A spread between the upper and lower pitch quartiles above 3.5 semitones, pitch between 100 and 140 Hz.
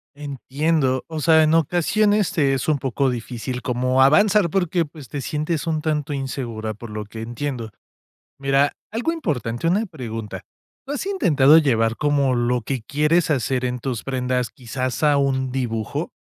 Yes: average, 4.1 semitones; low, 135 Hz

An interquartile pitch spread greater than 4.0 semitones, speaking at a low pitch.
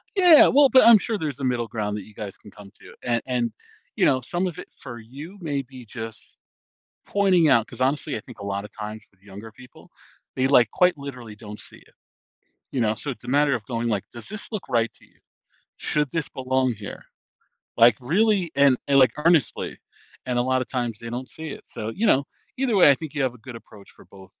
Yes: average, 4.9 semitones; low, 130 Hz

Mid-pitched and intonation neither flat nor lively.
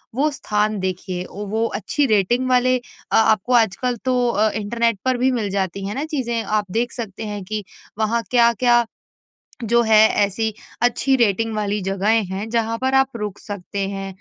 No: high, 220 Hz; average, 3.0 semitones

